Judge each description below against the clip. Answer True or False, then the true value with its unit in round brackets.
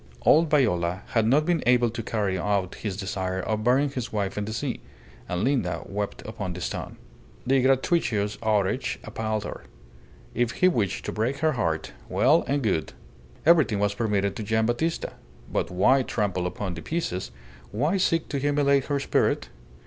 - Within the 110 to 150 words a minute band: False (170 wpm)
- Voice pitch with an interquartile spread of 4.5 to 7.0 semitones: True (5.5 semitones)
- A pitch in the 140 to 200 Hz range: False (110 Hz)